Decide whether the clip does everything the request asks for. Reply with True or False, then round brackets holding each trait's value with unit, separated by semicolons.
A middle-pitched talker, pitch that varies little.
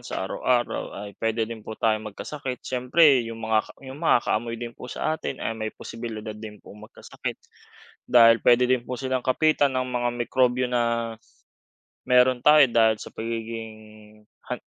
False (120 Hz; 2.2 semitones)